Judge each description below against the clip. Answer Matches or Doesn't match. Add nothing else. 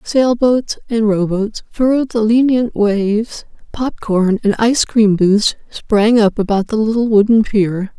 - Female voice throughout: Matches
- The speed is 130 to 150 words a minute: Matches